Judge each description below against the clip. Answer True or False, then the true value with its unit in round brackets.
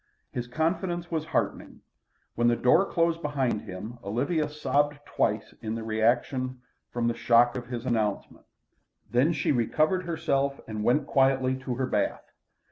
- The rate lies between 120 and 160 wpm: True (150 wpm)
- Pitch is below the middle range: True (130 Hz)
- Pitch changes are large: False (4.1 semitones)